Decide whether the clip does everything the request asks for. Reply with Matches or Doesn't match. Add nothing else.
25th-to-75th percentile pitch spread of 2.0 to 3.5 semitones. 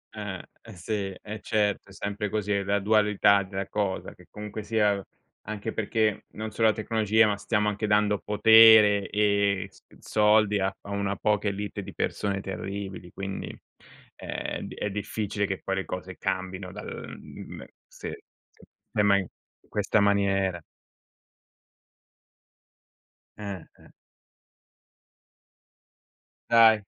Doesn't match